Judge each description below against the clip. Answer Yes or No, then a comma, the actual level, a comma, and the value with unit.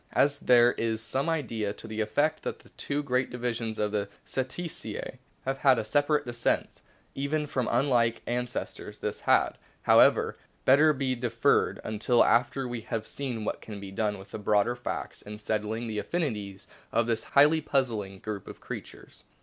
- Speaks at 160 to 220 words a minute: Yes, average, 175 wpm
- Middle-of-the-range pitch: No, low, 120 Hz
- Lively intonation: No, average, 3.9 semitones